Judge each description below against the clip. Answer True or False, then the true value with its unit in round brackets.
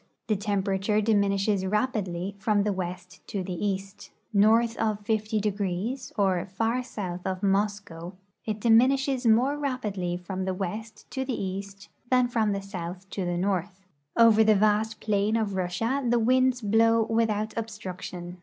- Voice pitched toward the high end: True (205 Hz)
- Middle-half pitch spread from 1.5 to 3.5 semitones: True (2.9 semitones)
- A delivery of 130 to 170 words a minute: True (155 wpm)